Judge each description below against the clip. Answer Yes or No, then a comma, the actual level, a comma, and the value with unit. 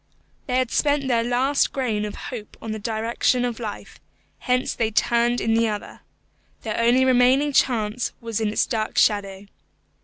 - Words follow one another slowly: No, average, 165 wpm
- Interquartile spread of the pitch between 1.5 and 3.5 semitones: Yes, narrow, 2.5 semitones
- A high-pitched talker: Yes, high, 235 Hz